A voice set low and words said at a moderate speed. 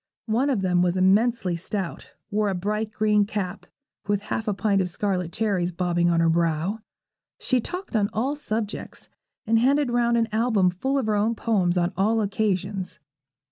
No: high, 205 Hz; average, 180 wpm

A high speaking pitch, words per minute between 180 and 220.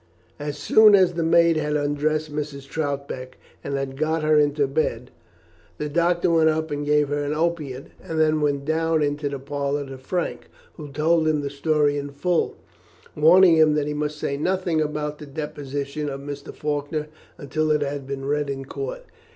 No: medium, 150 Hz; average, 185 wpm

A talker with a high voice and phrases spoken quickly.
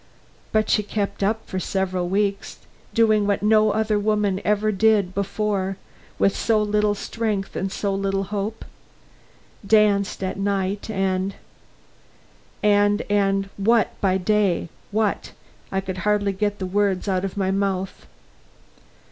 No: high, 200 Hz; average, 140 wpm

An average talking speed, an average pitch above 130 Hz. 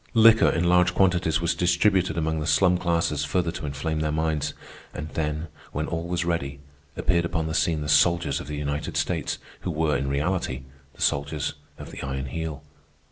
No: average, 190 wpm; very low, 80 Hz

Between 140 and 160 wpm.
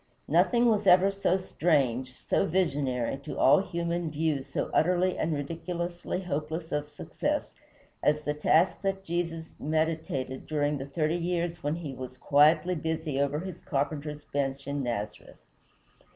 Yes: average, 145 wpm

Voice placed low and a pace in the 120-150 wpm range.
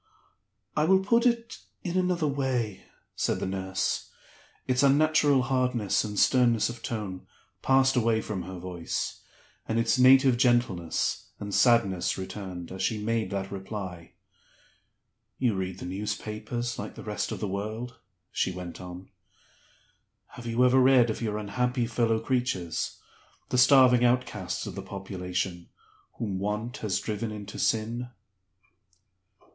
Yes: low, 115 Hz; average, 140 wpm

